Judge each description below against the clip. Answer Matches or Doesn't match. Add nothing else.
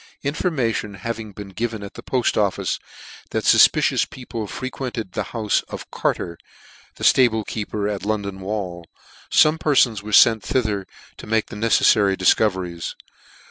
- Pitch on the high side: Doesn't match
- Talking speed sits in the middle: Matches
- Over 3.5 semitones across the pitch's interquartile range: Doesn't match